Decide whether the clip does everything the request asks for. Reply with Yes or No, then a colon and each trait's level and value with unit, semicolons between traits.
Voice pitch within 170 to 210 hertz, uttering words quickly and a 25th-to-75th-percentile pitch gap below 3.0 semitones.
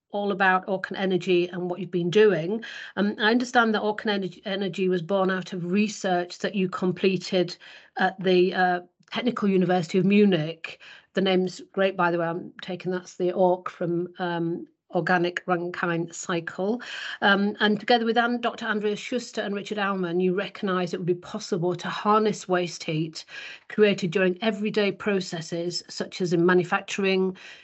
No: high, 190 Hz; average, 165 wpm; narrow, 2.5 semitones